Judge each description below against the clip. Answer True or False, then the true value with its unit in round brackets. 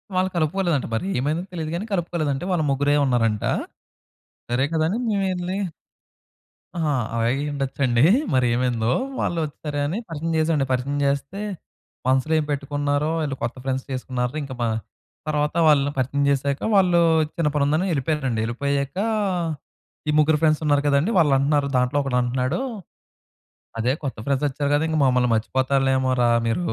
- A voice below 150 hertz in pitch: True (140 Hz)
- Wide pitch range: False (3.2 semitones)